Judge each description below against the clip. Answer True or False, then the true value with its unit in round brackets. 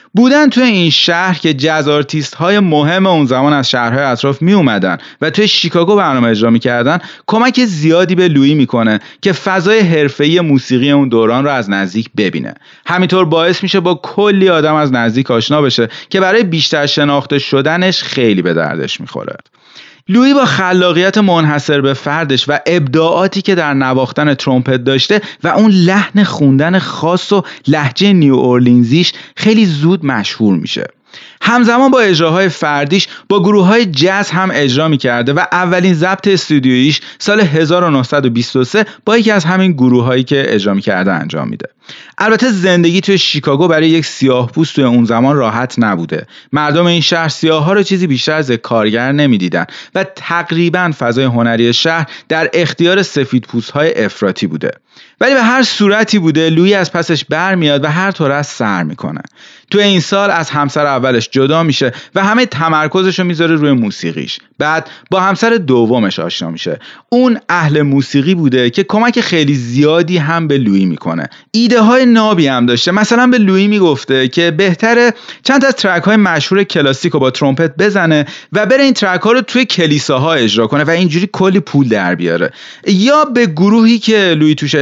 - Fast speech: True (170 wpm)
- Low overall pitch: False (165 Hz)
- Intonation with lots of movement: True (5.8 semitones)